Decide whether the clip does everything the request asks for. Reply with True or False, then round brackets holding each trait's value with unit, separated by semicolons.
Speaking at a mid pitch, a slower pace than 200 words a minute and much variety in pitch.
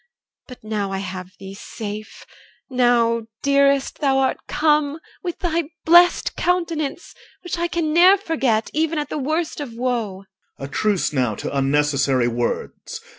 False (255 Hz; 150 wpm; 8.3 semitones)